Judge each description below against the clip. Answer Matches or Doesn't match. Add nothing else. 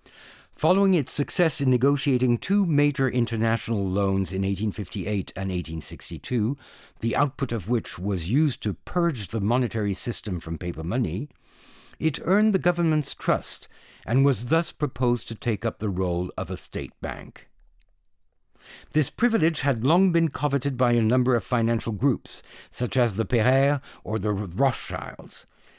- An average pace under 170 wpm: Matches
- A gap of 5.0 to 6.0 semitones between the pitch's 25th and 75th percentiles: Matches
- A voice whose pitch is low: Matches